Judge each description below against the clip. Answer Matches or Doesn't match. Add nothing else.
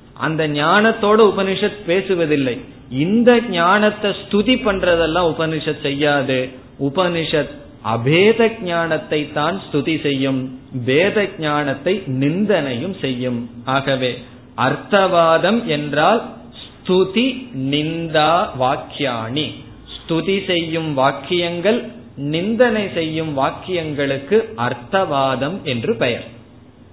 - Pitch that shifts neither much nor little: Doesn't match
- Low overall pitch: Doesn't match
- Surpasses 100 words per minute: Doesn't match